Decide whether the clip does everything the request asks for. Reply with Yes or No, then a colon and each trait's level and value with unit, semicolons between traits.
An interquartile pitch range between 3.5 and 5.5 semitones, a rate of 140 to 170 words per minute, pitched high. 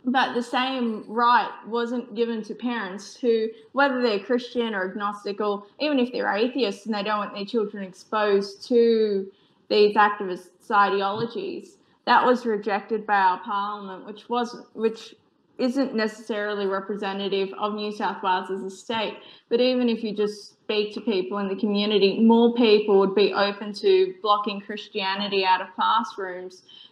No: average, 2.8 semitones; average, 160 wpm; high, 210 Hz